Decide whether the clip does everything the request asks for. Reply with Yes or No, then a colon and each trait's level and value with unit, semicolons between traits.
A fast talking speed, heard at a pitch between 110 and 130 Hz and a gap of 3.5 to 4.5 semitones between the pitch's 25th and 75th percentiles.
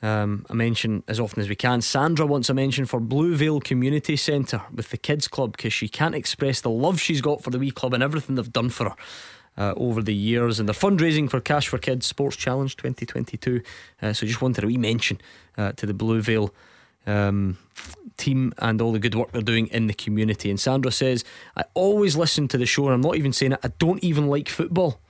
Yes: fast, 225 wpm; low, 125 Hz; average, 4.2 semitones